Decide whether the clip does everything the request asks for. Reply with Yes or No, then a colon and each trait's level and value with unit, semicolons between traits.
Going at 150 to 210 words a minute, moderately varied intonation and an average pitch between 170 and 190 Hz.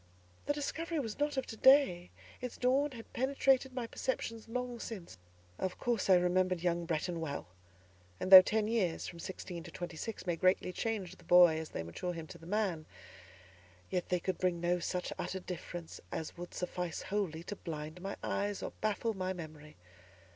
Yes: average, 185 wpm; average, 4.8 semitones; medium, 185 Hz